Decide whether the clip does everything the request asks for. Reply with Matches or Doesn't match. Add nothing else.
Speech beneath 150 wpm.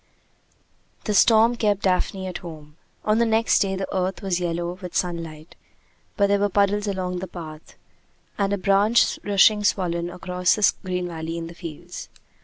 Doesn't match